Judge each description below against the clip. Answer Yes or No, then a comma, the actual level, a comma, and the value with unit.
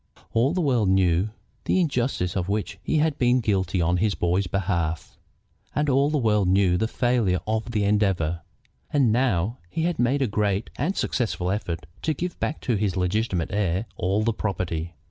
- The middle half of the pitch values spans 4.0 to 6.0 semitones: Yes, average, 5.3 semitones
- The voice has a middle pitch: No, low, 105 Hz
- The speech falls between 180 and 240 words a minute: Yes, average, 185 wpm